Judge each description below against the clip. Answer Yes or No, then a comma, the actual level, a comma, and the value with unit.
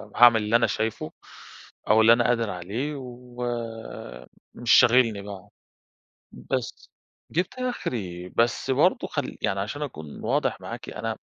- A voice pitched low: Yes, low, 115 Hz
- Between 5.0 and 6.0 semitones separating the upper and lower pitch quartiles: No, average, 3.3 semitones